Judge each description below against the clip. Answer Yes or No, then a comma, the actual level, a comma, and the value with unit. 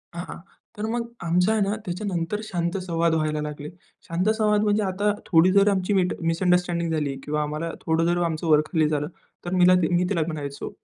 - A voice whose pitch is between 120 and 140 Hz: No, medium, 170 Hz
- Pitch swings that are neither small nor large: Yes, average, 3.0 semitones